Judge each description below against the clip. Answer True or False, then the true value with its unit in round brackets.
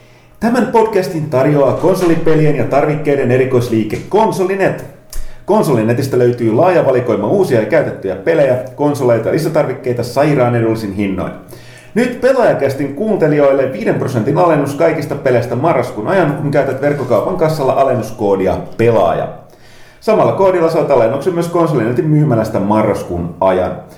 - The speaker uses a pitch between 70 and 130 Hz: False (140 Hz)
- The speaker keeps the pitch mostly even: False (5.2 semitones)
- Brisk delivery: False (115 wpm)